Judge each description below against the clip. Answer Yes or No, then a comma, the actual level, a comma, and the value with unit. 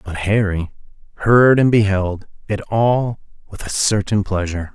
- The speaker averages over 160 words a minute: No, average, 140 wpm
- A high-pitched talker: No, low, 105 Hz